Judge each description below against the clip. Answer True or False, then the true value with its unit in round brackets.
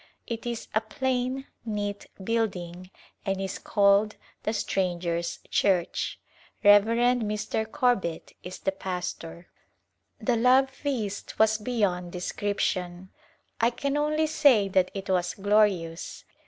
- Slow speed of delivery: True (120 wpm)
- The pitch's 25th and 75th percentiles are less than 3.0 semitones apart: False (4.2 semitones)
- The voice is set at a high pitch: True (205 Hz)